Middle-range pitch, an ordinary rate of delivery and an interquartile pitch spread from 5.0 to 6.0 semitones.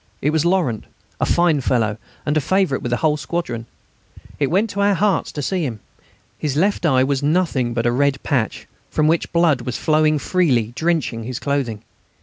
Yes: medium, 145 Hz; average, 190 wpm; wide, 5.4 semitones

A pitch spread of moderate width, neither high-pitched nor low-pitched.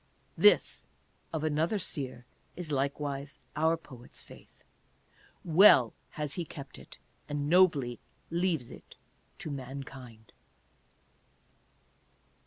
Yes: average, 3.5 semitones; medium, 145 Hz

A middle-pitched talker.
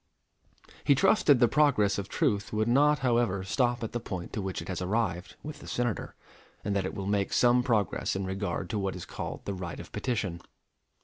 No: low, 105 Hz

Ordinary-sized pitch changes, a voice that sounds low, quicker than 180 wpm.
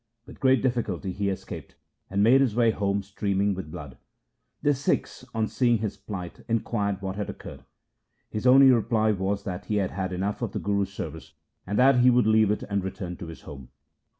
Yes: average, 3.3 semitones; low, 100 Hz; average, 200 wpm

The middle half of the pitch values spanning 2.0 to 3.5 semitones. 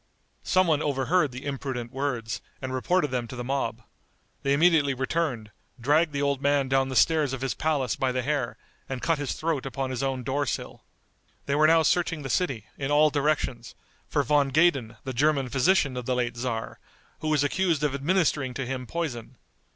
Yes: average, 2.9 semitones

